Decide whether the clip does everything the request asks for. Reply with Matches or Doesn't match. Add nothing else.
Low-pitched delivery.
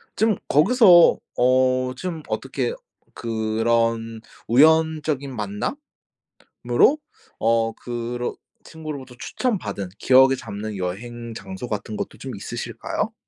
Matches